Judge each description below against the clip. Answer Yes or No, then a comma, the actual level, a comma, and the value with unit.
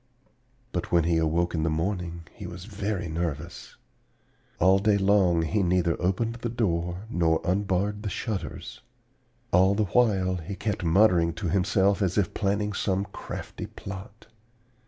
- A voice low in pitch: Yes, very low, 95 Hz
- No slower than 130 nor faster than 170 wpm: Yes, average, 150 wpm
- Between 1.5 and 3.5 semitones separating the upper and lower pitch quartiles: Yes, average, 3.1 semitones